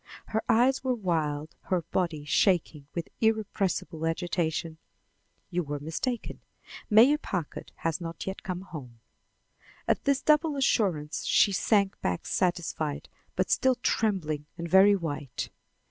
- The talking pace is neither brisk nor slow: No, slow, 130 wpm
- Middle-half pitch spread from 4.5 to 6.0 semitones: Yes, wide, 5.6 semitones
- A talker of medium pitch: Yes, medium, 175 Hz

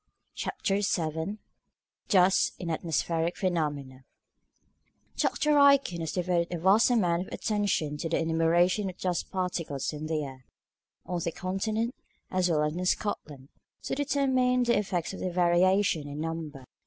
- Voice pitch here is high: No, medium, 175 Hz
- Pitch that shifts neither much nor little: Yes, average, 3.5 semitones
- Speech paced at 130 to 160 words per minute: Yes, average, 145 wpm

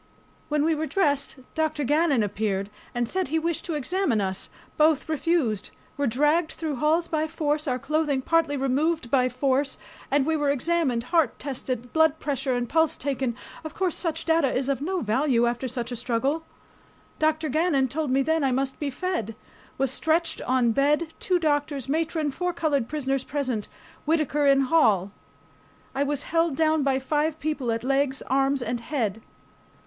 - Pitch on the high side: Yes, very high, 285 Hz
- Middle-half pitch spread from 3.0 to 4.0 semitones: Yes, average, 3.6 semitones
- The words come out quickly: No, average, 175 wpm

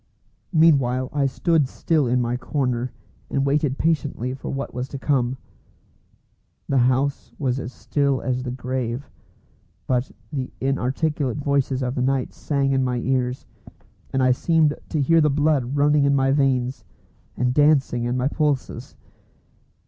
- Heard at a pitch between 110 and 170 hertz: Yes, low, 135 Hz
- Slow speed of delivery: No, average, 150 wpm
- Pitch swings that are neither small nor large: No, narrow, 2.3 semitones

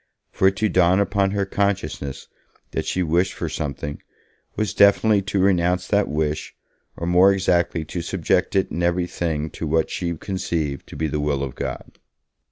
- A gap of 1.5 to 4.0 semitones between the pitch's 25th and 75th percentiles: Yes, average, 3.7 semitones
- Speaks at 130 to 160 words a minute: No, average, 175 wpm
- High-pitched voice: No, very low, 90 Hz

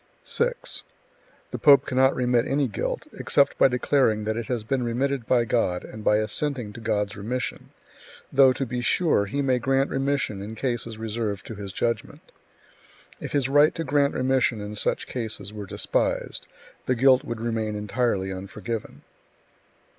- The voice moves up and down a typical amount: Yes, average, 3.8 semitones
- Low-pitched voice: Yes, low, 120 Hz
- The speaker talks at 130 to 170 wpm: Yes, average, 160 wpm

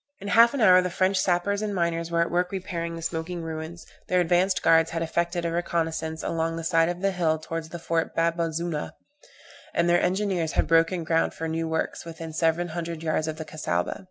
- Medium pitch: Yes, medium, 170 Hz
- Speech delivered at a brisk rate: Yes, fast, 215 wpm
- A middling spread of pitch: No, narrow, 1.5 semitones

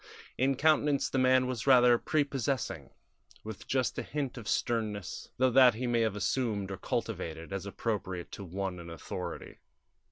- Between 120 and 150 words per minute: No, average, 160 wpm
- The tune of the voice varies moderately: Yes, average, 4.9 semitones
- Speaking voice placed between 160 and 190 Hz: No, low, 115 Hz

